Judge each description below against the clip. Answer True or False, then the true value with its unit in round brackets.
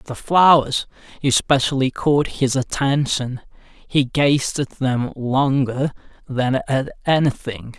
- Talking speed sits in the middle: False (110 wpm)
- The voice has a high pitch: False (135 Hz)